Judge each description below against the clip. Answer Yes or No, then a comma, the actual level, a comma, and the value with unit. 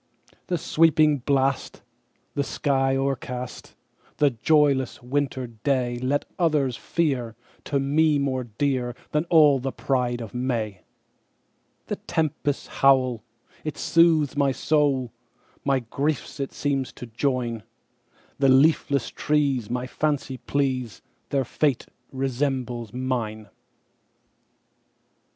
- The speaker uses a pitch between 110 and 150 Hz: Yes, low, 135 Hz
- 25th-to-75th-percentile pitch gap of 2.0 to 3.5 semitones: Yes, average, 2.8 semitones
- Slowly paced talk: Yes, slow, 90 wpm